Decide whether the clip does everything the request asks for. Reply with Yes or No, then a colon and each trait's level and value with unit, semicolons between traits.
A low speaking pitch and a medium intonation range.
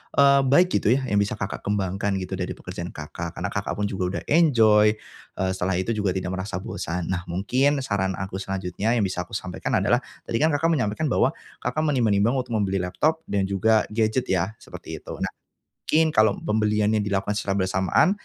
Yes: low, 105 Hz; average, 3.9 semitones